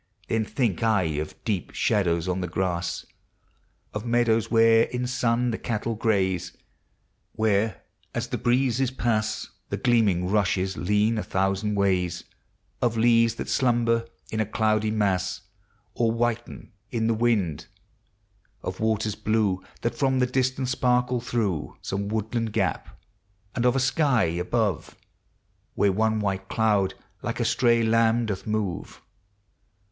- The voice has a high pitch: No, low, 110 Hz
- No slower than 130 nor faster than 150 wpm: Yes, average, 140 wpm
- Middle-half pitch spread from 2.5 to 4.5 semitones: Yes, average, 3.3 semitones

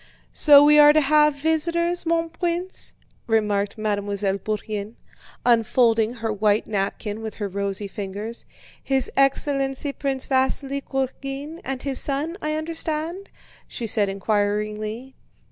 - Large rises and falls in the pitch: Yes, wide, 6.0 semitones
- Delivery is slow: Yes, slow, 125 wpm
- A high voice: Yes, very high, 260 Hz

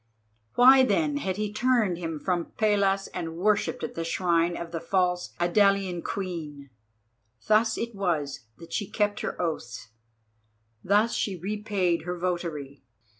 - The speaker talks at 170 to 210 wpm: No, average, 140 wpm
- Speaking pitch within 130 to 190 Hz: Yes, medium, 185 Hz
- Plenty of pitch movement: No, average, 3.9 semitones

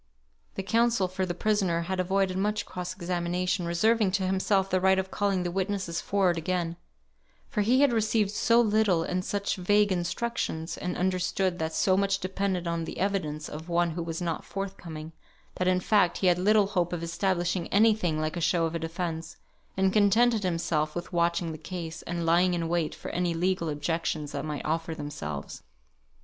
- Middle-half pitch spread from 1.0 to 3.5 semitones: Yes, average, 2.7 semitones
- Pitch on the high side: No, medium, 180 Hz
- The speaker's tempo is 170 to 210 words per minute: Yes, average, 190 wpm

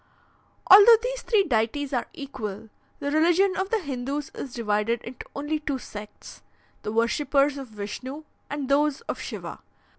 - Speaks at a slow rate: No, average, 150 wpm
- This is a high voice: Yes, very high, 280 Hz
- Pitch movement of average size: Yes, average, 5.0 semitones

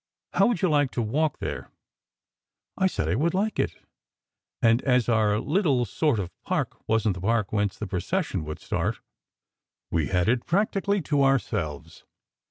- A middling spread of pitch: No, wide, 7.6 semitones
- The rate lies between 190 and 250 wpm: No, average, 175 wpm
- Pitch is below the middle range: Yes, low, 120 Hz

